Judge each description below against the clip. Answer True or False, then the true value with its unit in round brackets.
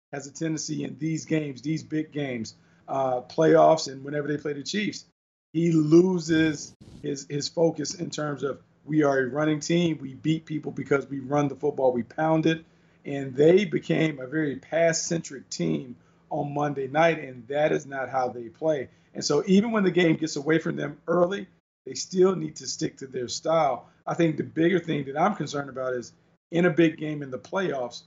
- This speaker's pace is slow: False (200 wpm)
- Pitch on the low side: False (155 Hz)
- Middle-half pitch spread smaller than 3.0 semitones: True (2.6 semitones)